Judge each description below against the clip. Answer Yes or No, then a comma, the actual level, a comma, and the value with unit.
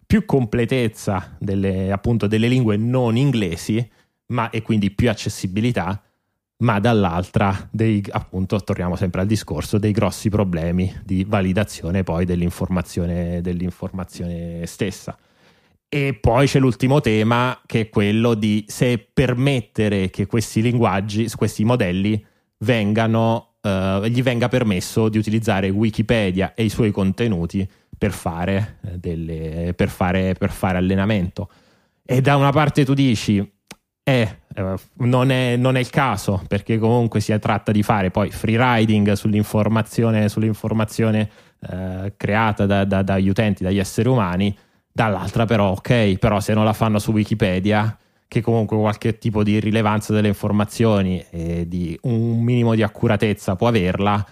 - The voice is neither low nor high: No, low, 105 Hz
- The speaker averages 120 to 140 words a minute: Yes, average, 135 wpm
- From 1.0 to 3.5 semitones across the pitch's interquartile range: Yes, average, 3.0 semitones